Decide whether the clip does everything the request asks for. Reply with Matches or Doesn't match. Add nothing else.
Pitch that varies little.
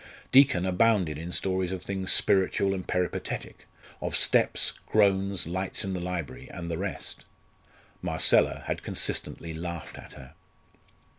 Matches